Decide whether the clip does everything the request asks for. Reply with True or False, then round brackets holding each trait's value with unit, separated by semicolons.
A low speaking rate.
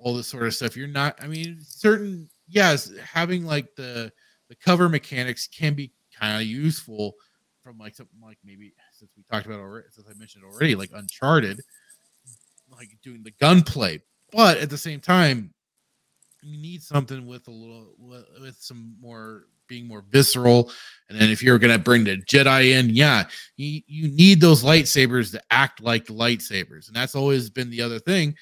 False (180 wpm)